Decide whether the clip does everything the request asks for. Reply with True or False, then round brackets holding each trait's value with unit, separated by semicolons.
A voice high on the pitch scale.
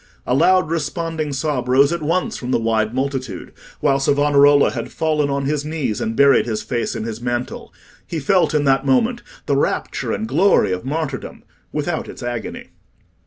False (140 Hz)